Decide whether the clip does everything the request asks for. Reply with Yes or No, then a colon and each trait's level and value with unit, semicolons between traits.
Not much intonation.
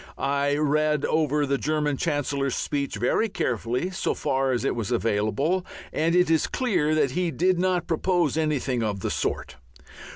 No: average, 3.5 semitones